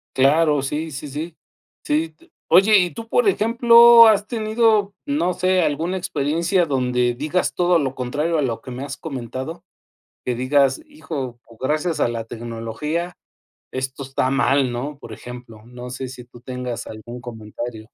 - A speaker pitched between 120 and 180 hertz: Yes, medium, 140 Hz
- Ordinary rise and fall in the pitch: No, wide, 6.0 semitones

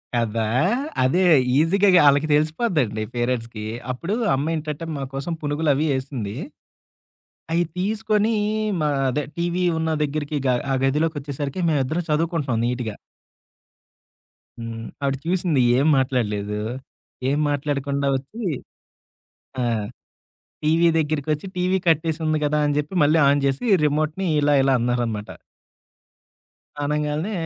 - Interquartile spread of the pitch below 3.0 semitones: No, average, 3.4 semitones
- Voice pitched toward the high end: No, medium, 145 Hz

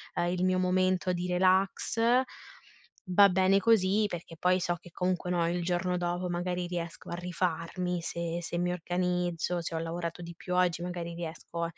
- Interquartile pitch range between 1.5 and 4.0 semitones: No, narrow, 1.1 semitones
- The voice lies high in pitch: No, medium, 180 Hz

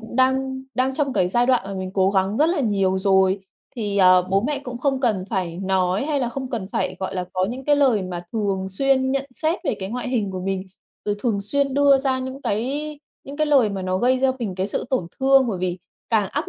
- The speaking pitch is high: Yes, high, 230 Hz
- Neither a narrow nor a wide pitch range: No, wide, 5.8 semitones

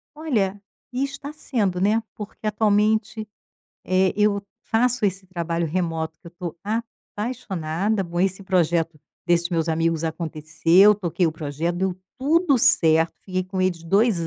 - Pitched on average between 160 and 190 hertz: Yes, medium, 185 Hz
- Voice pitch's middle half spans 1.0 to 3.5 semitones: No, average, 4.2 semitones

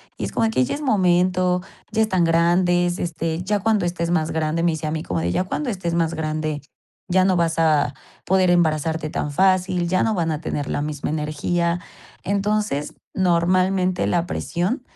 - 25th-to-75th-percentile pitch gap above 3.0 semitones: No, average, 2.7 semitones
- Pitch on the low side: No, medium, 175 Hz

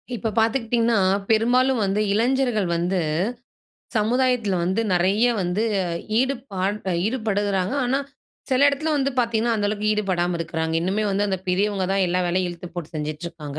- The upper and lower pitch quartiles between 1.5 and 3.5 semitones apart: No, average, 4.5 semitones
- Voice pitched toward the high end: Yes, high, 205 Hz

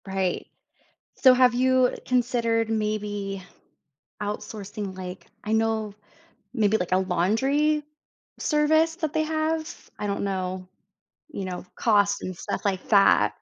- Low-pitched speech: No, high, 215 Hz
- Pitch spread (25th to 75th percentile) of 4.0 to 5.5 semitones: Yes, average, 4.9 semitones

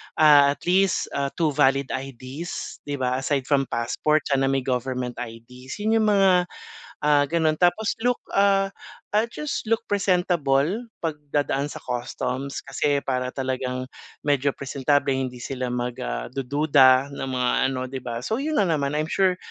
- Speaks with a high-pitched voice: No, medium, 140 Hz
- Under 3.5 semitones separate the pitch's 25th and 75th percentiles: No, average, 3.9 semitones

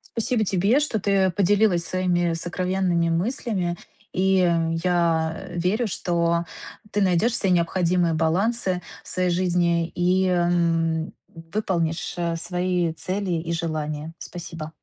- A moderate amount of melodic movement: No, narrow, 2.1 semitones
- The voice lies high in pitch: No, medium, 175 Hz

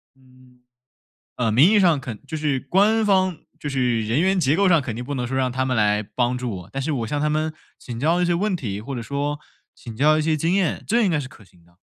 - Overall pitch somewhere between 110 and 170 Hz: Yes, medium, 140 Hz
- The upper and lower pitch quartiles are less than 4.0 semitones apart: No, average, 5.0 semitones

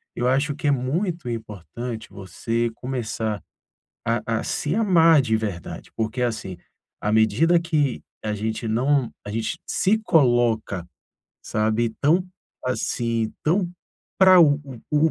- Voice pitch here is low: Yes, low, 120 Hz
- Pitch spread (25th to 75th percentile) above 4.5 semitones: Yes, wide, 5.4 semitones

